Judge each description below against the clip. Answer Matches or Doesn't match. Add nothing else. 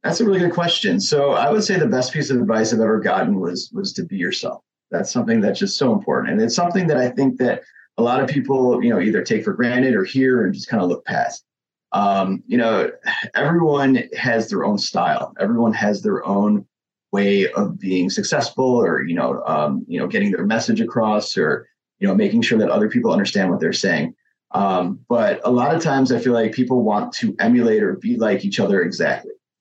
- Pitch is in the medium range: Matches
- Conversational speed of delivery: Doesn't match